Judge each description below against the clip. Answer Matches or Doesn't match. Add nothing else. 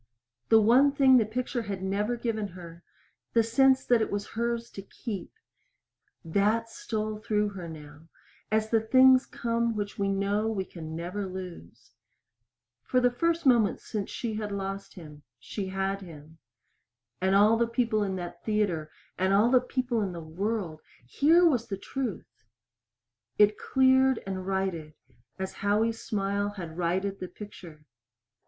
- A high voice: Matches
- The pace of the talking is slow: Doesn't match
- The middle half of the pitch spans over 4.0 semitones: Doesn't match